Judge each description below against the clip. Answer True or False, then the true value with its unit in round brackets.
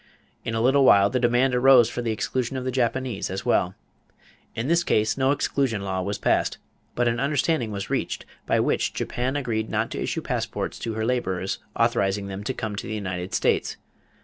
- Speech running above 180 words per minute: True (200 wpm)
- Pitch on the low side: True (115 Hz)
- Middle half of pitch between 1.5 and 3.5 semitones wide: False (4.2 semitones)